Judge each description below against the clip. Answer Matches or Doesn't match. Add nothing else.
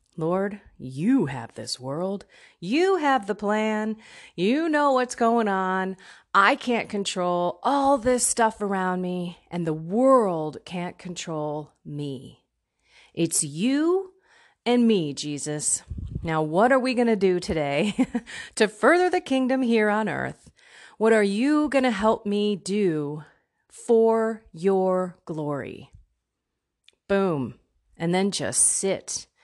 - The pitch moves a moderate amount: Doesn't match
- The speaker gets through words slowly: Matches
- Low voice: Doesn't match